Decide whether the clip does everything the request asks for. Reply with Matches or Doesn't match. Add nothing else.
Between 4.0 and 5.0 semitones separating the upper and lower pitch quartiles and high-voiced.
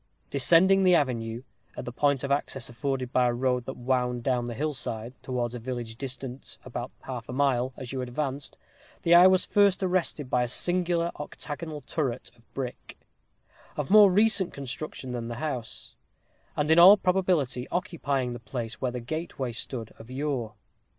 Doesn't match